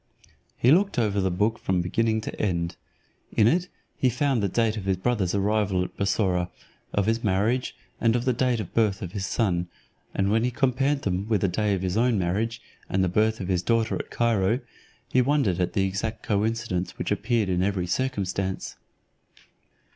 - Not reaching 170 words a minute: No, average, 185 wpm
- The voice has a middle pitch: No, low, 105 Hz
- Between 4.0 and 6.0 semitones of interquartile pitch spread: No, average, 3.6 semitones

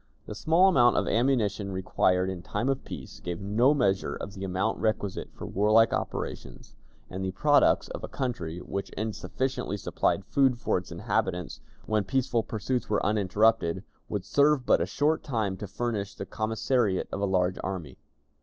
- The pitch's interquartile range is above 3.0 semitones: Yes, average, 4.5 semitones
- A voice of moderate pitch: No, low, 105 Hz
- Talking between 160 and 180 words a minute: Yes, average, 170 wpm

